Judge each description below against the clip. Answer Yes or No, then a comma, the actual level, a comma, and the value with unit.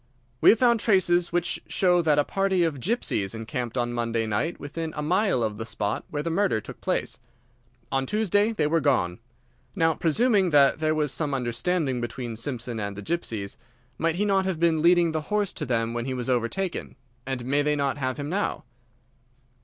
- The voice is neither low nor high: Yes, medium, 150 Hz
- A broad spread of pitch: Yes, wide, 6.6 semitones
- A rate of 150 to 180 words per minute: No, average, 195 wpm